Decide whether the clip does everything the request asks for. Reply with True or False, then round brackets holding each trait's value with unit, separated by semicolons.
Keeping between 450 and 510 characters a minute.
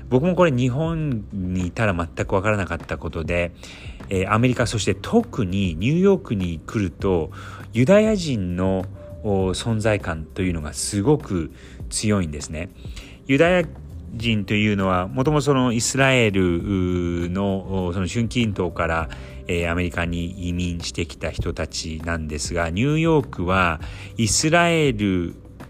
False (290 characters per minute)